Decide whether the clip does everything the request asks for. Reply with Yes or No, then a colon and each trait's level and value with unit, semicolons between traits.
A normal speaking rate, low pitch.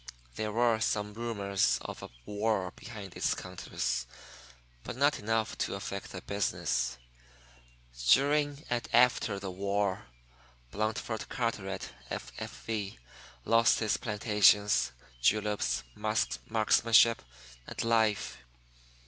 No: slow, 100 wpm; low, 105 Hz